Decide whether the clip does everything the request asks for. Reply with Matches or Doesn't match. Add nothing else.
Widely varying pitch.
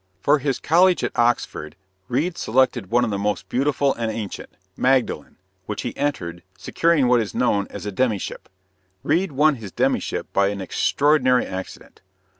Matches